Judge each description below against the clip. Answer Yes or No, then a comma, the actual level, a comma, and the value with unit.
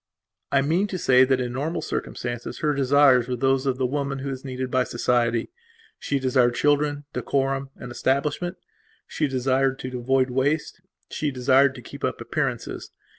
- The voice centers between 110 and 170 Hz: Yes, low, 135 Hz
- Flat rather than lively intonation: Yes, narrow, 1.9 semitones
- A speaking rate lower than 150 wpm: No, average, 170 wpm